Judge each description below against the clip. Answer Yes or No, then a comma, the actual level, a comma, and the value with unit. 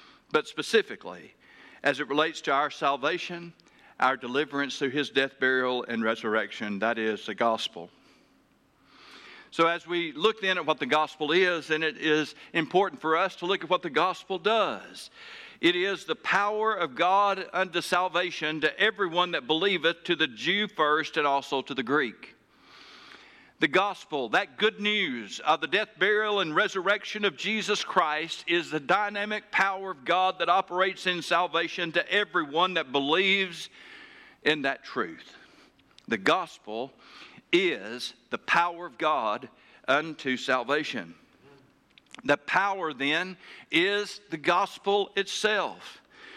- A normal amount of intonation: Yes, average, 4.9 semitones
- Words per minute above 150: No, average, 145 wpm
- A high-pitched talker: No, medium, 175 Hz